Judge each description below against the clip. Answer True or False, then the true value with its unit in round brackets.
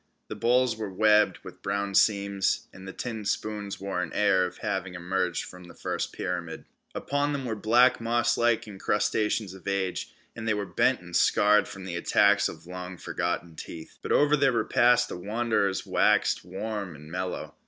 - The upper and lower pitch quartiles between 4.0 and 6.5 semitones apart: False (3.5 semitones)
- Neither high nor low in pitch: False (100 Hz)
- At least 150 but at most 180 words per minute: True (175 wpm)